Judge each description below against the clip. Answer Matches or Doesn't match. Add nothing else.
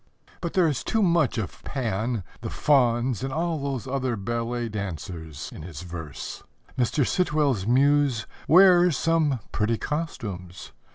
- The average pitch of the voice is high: Doesn't match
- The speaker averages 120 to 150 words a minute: Matches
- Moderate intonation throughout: Doesn't match